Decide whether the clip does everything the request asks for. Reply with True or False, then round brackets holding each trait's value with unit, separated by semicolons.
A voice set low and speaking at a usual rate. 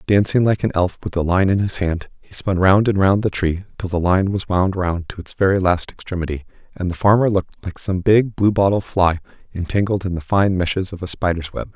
False (95 Hz; 235 wpm)